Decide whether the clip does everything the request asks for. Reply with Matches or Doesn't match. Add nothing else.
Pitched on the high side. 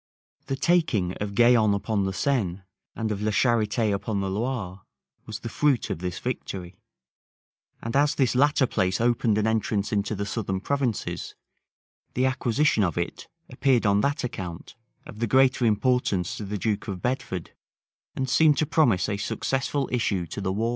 Doesn't match